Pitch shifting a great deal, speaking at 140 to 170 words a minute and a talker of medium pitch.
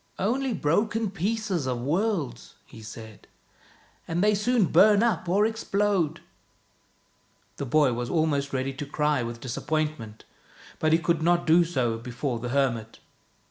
Yes: wide, 7.9 semitones; average, 155 wpm; medium, 155 Hz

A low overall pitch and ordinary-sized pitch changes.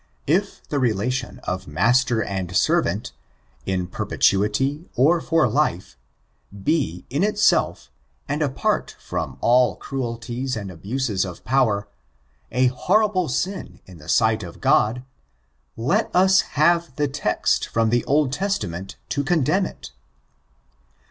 No: low, 125 Hz; wide, 7.0 semitones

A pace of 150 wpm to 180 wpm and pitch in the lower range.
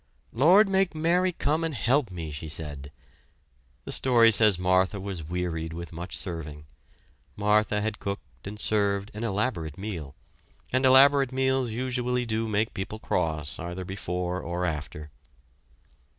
No: average, 140 wpm; low, 100 Hz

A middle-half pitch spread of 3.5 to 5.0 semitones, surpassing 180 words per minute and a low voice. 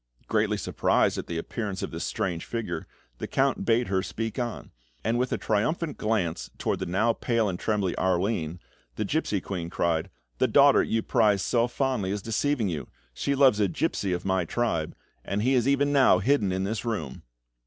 Yes: average, 4.5 semitones; average, 190 wpm; low, 105 Hz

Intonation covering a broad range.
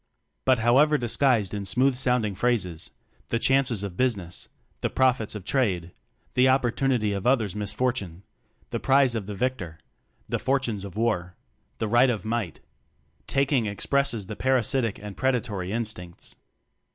No: average, 4.3 semitones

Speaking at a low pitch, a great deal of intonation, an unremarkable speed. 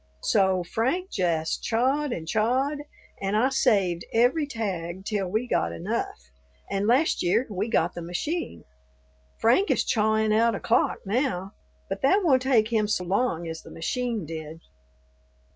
No: high, 215 Hz; wide, 5.8 semitones; average, 155 wpm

